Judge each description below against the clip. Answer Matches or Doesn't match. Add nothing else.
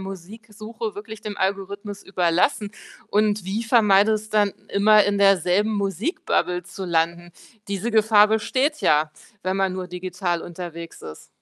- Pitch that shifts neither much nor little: Matches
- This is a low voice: Doesn't match